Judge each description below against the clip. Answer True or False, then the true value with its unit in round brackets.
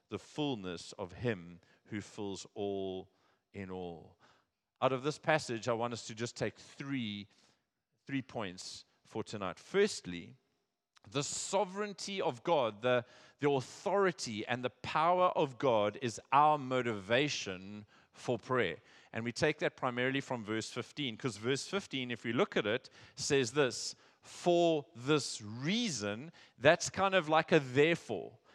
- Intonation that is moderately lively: False (6.0 semitones)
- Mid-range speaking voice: False (125 Hz)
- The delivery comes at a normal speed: True (145 wpm)